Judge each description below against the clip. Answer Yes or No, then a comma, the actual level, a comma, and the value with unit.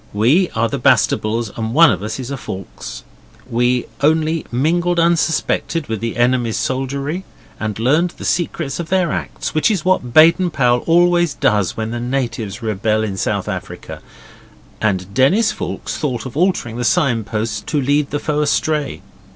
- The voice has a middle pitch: No, low, 130 Hz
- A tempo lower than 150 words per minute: No, average, 165 wpm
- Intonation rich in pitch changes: Yes, wide, 6.2 semitones